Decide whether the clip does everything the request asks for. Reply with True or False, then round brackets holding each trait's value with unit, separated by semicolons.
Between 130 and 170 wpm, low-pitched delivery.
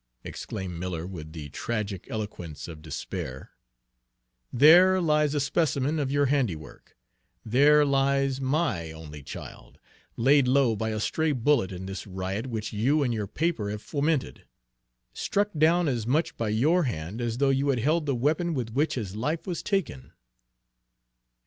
True (155 wpm; 125 Hz)